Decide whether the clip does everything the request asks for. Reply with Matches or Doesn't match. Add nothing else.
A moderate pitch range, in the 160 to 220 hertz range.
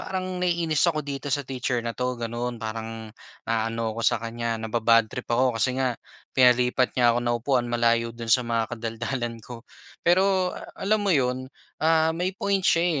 Doesn't match